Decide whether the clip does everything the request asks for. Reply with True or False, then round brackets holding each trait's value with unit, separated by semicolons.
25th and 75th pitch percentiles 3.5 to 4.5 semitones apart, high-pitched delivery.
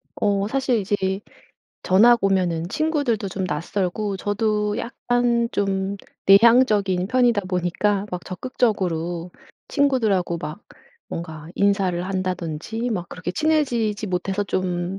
True (4.0 semitones; 200 Hz)